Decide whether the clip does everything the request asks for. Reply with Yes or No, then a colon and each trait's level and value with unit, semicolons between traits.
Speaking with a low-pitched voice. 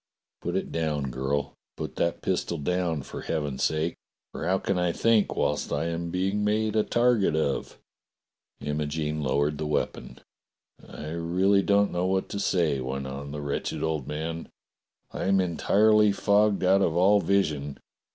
Yes: very low, 85 Hz